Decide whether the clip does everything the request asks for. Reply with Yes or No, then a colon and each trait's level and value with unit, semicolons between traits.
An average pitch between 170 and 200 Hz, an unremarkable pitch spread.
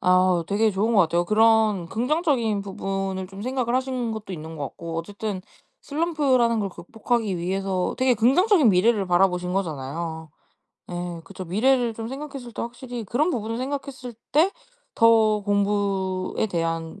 No: high, 210 Hz; average, 4.8 semitones